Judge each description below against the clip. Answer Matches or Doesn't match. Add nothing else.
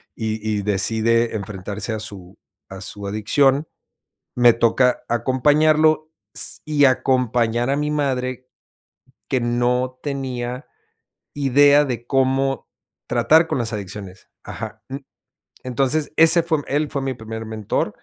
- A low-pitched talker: Matches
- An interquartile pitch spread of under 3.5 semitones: Doesn't match